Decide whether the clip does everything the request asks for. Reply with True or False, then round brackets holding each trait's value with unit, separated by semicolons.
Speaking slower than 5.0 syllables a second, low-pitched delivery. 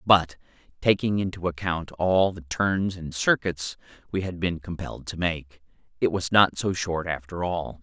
True (4.5 syllables/s; 90 Hz)